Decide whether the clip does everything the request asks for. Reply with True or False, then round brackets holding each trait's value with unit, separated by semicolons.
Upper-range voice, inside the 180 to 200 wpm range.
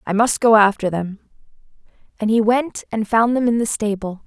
True (220 Hz; 195 wpm)